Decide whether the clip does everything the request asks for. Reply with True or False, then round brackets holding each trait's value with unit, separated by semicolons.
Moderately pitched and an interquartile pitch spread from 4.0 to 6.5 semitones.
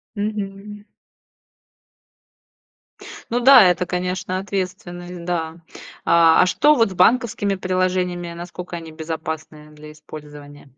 False (180 Hz; 3.3 semitones)